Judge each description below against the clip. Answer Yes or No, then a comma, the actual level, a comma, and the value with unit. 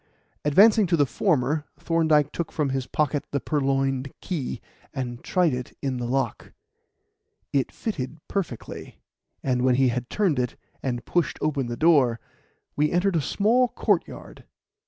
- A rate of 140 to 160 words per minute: Yes, average, 150 wpm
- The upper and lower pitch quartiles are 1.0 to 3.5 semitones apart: No, average, 4.6 semitones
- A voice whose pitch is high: No, medium, 140 Hz